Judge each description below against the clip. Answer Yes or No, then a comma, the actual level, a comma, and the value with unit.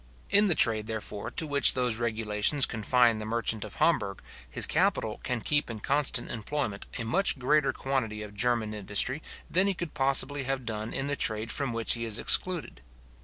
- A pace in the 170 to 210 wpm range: Yes, average, 185 wpm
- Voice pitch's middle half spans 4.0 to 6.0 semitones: Yes, average, 4.7 semitones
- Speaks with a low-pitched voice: Yes, low, 120 Hz